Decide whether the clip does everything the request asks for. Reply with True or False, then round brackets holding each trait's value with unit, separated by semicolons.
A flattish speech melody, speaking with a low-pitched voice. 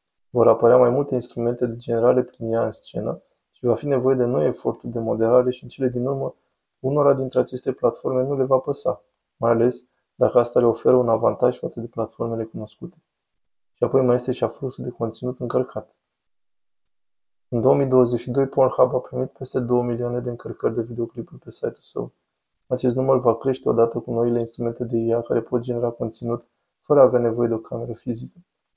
True (1.6 semitones; 125 Hz)